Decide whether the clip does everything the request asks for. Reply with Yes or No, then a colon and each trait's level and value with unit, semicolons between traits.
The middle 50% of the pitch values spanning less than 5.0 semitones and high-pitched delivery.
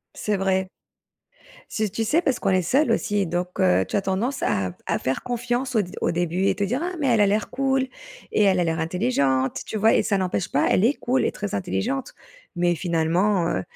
No: average, 5.3 semitones; high, 195 Hz